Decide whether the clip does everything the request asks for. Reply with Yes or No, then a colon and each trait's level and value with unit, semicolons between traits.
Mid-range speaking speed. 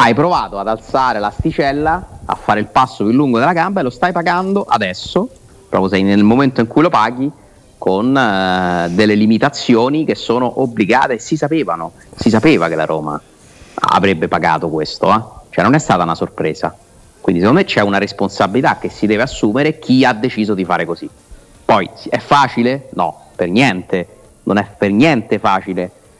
No: fast, 175 wpm